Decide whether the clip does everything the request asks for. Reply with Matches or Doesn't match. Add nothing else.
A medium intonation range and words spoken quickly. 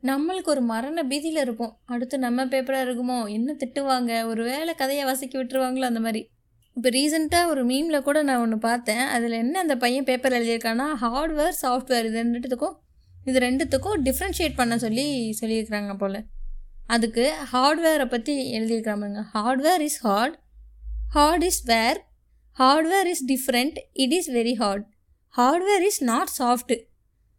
Matches